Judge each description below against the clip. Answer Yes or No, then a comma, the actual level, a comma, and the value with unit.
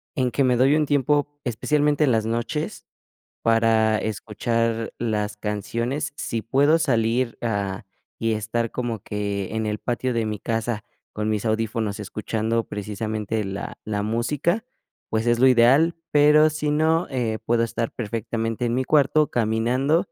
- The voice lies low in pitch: Yes, low, 115 Hz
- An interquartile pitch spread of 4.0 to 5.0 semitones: No, average, 3.6 semitones